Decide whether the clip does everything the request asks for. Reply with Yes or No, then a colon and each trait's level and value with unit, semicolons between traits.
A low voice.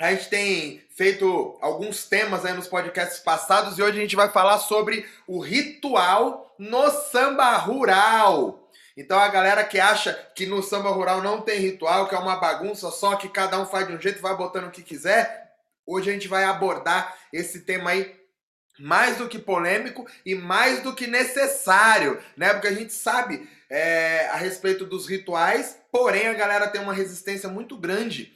No: high, 195 Hz